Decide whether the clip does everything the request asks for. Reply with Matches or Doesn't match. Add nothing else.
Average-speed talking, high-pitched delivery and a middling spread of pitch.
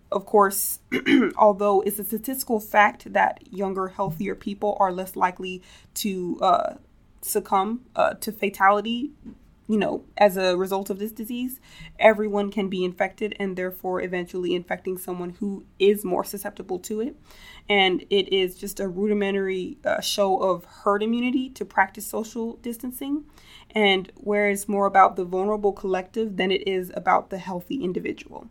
Doesn't match